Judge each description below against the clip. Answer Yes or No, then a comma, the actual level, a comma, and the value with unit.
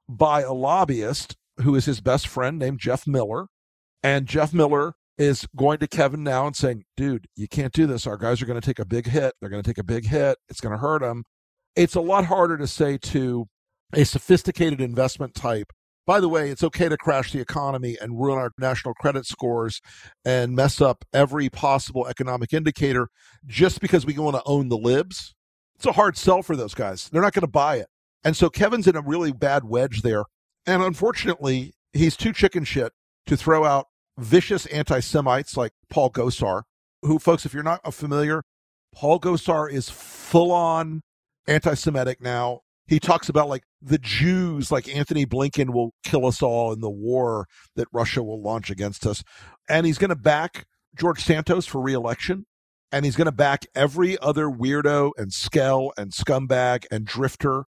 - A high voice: No, medium, 140 Hz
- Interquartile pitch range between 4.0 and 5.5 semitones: Yes, average, 4.3 semitones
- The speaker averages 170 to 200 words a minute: Yes, average, 190 wpm